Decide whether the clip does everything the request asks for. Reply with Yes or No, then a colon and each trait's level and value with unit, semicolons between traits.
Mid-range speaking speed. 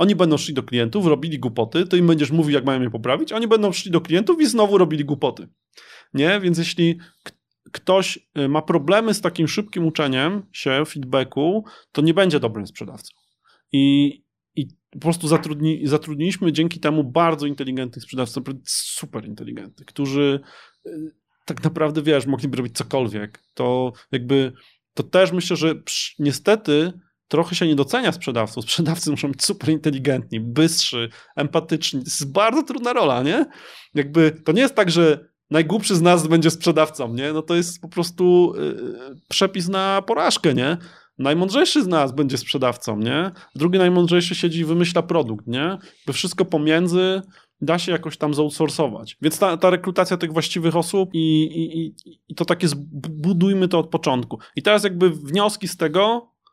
No: fast, 165 wpm